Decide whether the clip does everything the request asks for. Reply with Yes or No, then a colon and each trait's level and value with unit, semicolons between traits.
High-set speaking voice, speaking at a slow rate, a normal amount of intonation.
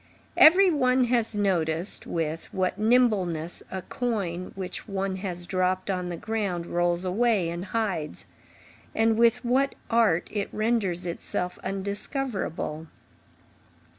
Yes: high, 195 Hz; slow, 120 wpm; average, 4.5 semitones